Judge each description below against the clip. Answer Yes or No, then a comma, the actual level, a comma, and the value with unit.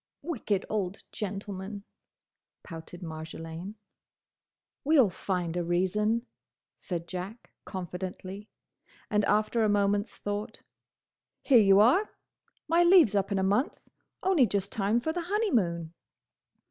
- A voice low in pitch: No, high, 205 Hz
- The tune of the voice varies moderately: Yes, average, 3.8 semitones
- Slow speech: Yes, slow, 120 wpm